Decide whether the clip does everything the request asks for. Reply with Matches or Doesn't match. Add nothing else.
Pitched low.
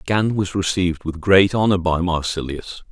Matches